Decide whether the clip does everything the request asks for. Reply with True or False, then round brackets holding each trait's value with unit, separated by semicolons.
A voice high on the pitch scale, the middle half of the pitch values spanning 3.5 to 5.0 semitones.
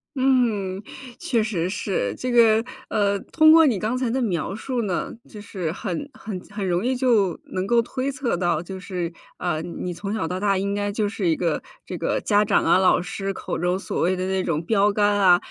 True (200 Hz; 3.9 semitones)